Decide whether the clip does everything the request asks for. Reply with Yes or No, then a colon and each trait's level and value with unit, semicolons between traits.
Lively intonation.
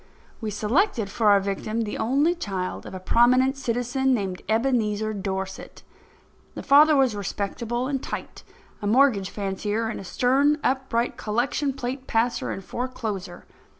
No: average, 4.3 semitones